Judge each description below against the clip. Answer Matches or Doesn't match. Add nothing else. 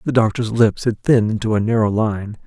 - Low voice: Matches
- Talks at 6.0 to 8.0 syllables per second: Doesn't match